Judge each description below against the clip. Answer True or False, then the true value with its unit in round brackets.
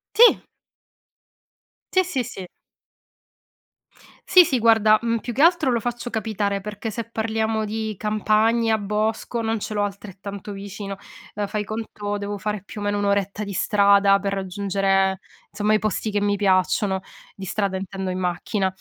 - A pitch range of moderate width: False (1.9 semitones)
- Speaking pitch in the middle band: False (210 Hz)